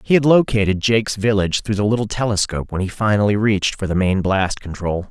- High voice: No, low, 105 Hz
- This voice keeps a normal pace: No, fast, 210 wpm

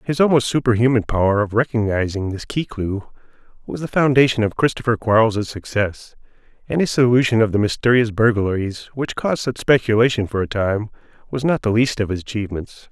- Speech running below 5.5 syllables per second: No, 5.7 syllables/s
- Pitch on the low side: Yes, low, 115 Hz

